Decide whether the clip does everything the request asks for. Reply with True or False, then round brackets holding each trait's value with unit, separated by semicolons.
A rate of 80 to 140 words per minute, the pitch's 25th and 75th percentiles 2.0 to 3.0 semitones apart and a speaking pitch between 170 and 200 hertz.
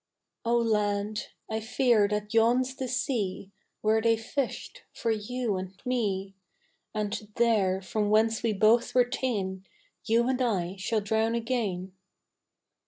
False (135 wpm; 2.7 semitones; 220 Hz)